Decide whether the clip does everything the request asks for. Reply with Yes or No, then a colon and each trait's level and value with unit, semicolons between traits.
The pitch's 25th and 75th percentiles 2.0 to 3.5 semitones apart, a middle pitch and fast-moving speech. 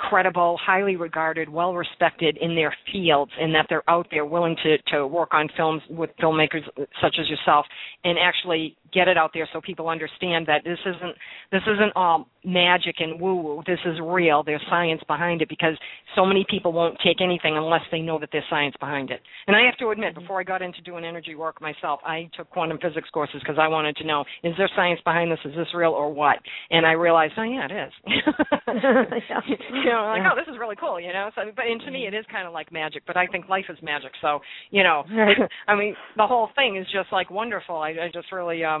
Yes: average, 3.2 semitones; medium, 170 Hz; fast, 230 wpm